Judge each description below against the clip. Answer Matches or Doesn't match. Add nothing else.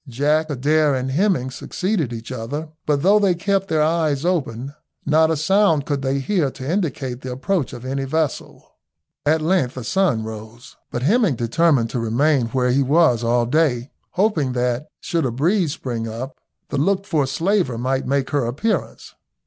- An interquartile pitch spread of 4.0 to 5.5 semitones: Matches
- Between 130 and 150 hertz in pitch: Matches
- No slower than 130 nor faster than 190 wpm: Matches